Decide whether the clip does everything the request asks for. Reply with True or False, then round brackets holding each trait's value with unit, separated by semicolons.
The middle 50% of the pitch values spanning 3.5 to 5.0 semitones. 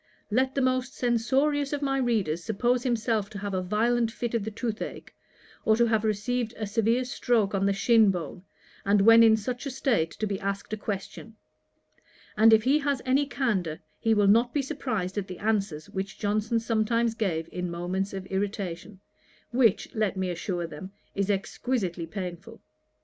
True (3.8 semitones)